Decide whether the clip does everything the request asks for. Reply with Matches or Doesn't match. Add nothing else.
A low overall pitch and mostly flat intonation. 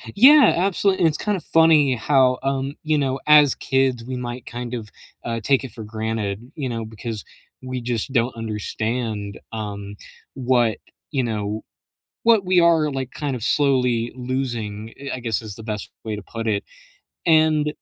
Doesn't match